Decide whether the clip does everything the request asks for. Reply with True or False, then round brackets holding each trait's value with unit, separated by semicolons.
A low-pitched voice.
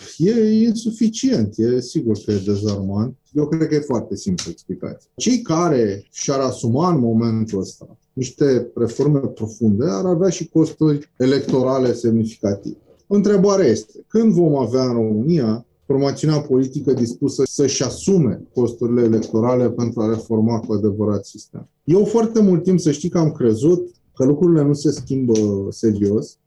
True (130 Hz)